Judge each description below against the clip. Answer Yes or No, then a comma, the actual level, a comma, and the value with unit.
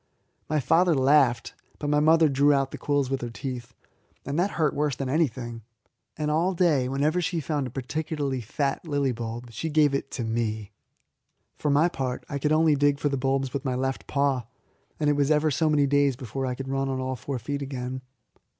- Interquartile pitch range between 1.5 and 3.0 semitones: Yes, narrow, 2.6 semitones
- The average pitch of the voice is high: No, medium, 140 Hz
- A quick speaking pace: Yes, fast, 210 wpm